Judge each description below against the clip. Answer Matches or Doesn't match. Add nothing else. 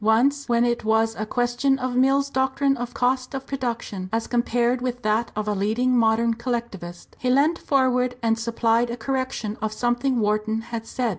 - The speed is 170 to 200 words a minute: Matches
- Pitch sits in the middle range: Doesn't match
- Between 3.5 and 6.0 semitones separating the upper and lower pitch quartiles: Doesn't match